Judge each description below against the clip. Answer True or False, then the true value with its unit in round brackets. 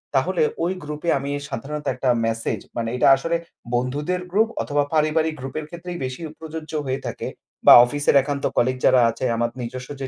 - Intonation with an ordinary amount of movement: True (3.6 semitones)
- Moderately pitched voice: True (145 Hz)